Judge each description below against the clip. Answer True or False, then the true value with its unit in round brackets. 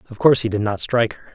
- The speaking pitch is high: False (110 Hz)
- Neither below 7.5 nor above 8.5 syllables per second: True (8.1 syllables/s)